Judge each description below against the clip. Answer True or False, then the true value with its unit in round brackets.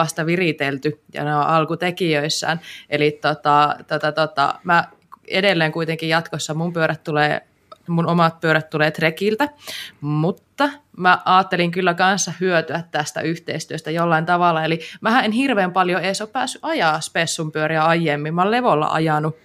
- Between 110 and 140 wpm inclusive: False (150 wpm)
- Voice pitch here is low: False (165 Hz)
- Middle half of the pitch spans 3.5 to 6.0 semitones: False (2.8 semitones)